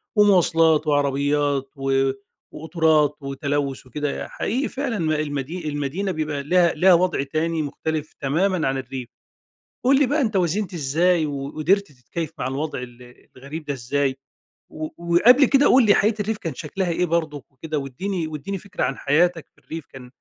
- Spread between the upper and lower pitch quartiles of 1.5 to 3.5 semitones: No, average, 4.4 semitones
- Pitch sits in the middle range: Yes, medium, 155 Hz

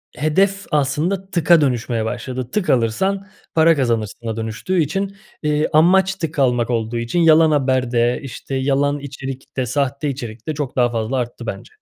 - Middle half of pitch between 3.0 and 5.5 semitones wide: Yes, average, 4.9 semitones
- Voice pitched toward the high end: No, low, 135 Hz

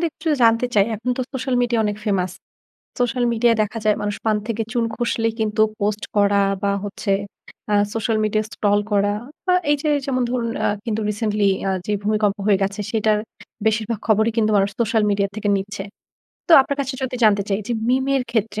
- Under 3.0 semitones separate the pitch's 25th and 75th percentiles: Yes, narrow, 2.4 semitones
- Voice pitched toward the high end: Yes, high, 215 Hz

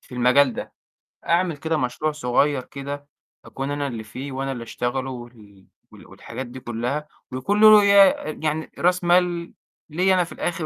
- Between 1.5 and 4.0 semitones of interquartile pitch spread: No, average, 5.2 semitones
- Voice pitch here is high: No, medium, 140 Hz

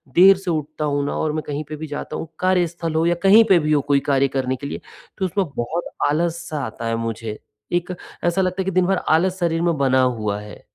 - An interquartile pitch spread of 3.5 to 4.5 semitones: Yes, average, 4.2 semitones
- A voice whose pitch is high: No, medium, 160 Hz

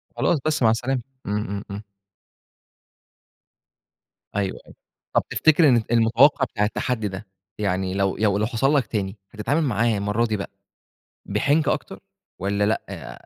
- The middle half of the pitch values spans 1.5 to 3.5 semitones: No, average, 4.2 semitones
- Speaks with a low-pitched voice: Yes, low, 110 Hz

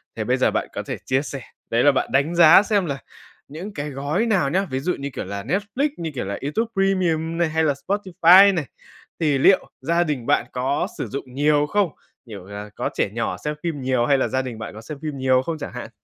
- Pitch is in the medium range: Yes, medium, 150 Hz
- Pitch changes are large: No, average, 4.9 semitones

